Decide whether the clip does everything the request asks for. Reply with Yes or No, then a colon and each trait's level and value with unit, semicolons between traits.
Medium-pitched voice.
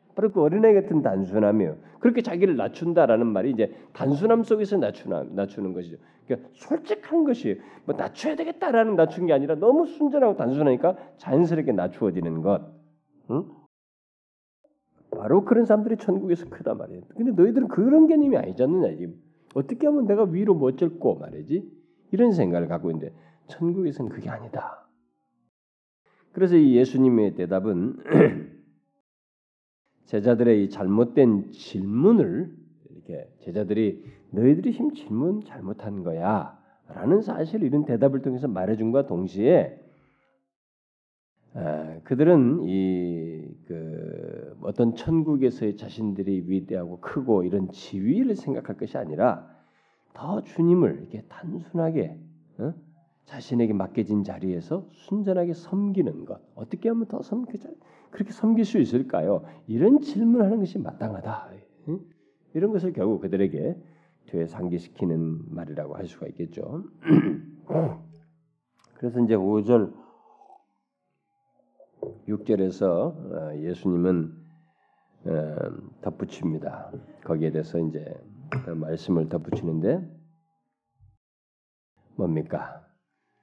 Yes: medium, 145 Hz